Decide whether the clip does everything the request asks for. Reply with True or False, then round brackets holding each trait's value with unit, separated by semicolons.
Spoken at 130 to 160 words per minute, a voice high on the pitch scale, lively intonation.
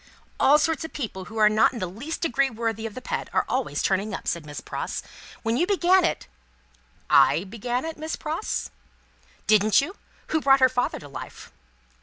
False (200 wpm; 240 Hz; 6.7 semitones)